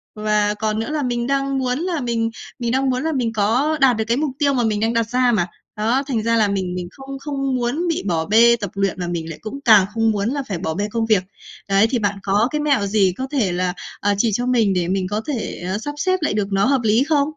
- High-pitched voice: Yes, high, 225 Hz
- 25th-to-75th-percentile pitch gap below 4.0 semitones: No, average, 4.7 semitones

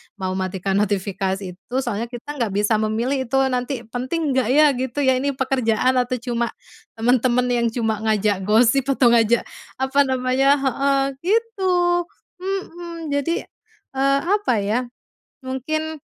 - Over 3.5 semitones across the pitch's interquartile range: Yes, average, 3.9 semitones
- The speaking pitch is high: Yes, very high, 255 Hz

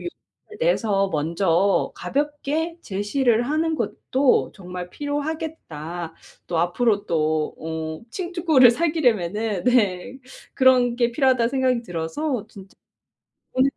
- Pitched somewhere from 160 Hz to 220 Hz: No, high, 235 Hz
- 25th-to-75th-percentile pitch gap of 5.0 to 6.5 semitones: No, wide, 8.0 semitones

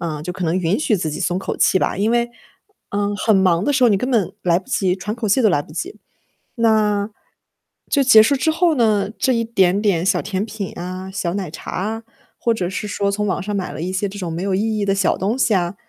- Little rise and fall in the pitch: No, average, 3.3 semitones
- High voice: Yes, high, 200 Hz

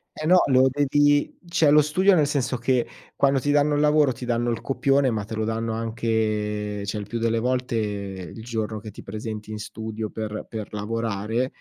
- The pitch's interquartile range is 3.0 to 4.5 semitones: Yes, average, 4.2 semitones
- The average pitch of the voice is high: No, low, 115 Hz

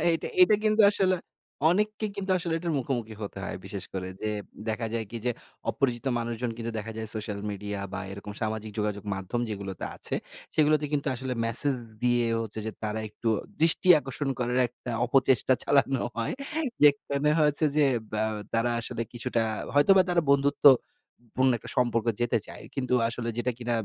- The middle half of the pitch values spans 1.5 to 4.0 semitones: No, average, 4.5 semitones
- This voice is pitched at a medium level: No, low, 120 Hz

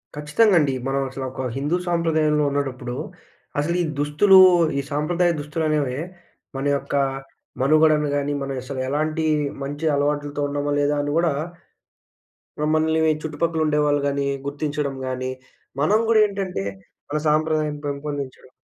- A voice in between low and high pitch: Yes, medium, 150 Hz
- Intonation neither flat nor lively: No, narrow, 2.0 semitones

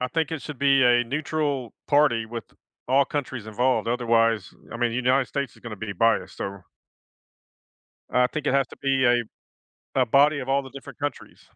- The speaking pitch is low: Yes, low, 130 Hz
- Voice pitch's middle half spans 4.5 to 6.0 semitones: No, average, 3.1 semitones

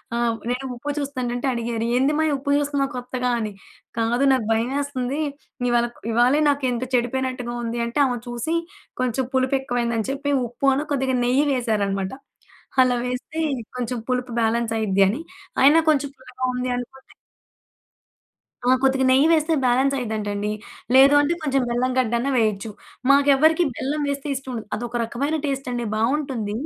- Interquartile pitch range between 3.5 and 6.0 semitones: No, average, 2.7 semitones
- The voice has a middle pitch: No, very high, 255 Hz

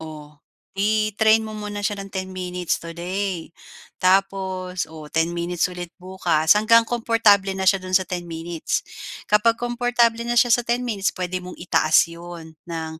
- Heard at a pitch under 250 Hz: Yes, medium, 185 Hz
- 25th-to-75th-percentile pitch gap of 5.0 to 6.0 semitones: No, average, 3.7 semitones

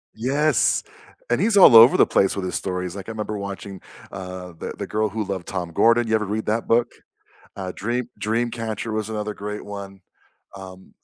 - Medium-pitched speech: No, low, 105 Hz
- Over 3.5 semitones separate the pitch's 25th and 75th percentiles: No, average, 2.8 semitones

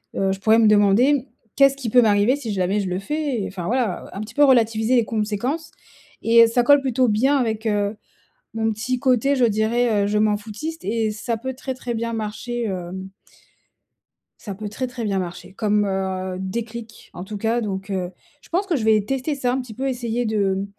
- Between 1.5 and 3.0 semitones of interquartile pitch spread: No, average, 3.5 semitones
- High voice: Yes, high, 225 Hz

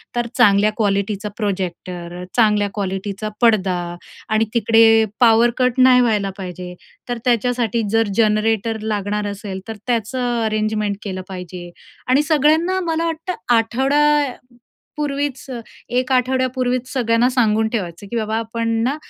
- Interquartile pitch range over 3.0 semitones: Yes, average, 3.5 semitones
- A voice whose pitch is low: No, high, 225 Hz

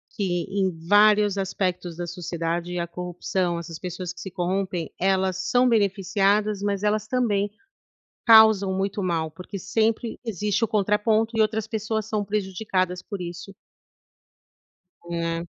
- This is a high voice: Yes, high, 195 Hz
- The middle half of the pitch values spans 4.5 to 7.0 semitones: No, average, 3.0 semitones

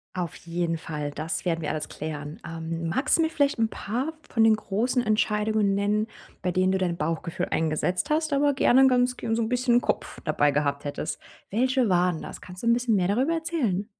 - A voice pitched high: Yes, high, 200 Hz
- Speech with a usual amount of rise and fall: No, wide, 6.9 semitones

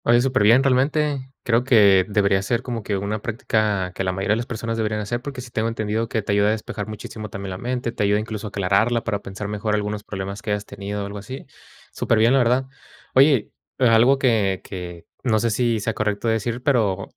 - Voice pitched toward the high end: No, low, 110 Hz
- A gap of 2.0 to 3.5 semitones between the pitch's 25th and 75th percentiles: Yes, average, 2.9 semitones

